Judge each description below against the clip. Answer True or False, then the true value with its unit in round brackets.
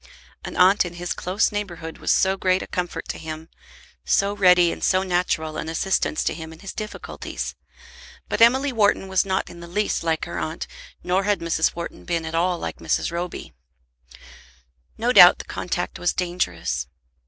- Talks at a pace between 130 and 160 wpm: False (180 wpm)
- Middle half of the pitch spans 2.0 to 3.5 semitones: True (2.9 semitones)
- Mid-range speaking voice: True (180 Hz)